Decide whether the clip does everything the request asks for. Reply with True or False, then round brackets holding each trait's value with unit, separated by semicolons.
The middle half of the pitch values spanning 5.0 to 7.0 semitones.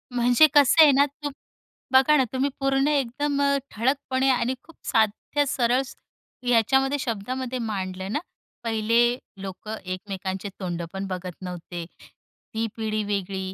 True (5.5 semitones)